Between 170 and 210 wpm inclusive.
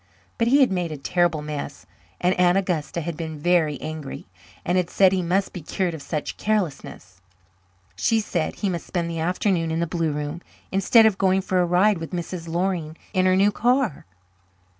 Yes: average, 195 wpm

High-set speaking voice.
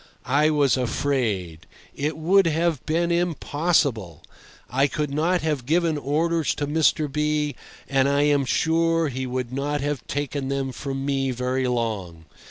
No: medium, 145 Hz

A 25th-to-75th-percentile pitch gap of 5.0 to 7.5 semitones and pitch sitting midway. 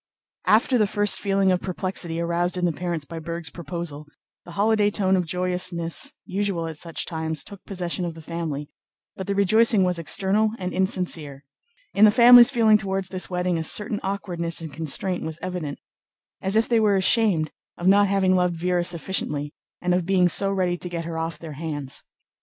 No: average, 2.9 semitones; medium, 180 Hz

